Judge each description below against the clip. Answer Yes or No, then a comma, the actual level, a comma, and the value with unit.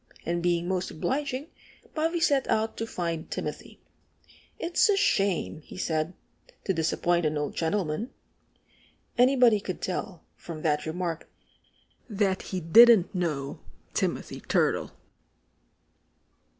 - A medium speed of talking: No, slow, 115 wpm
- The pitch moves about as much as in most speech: No, wide, 6.0 semitones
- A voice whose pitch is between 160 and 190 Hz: Yes, medium, 185 Hz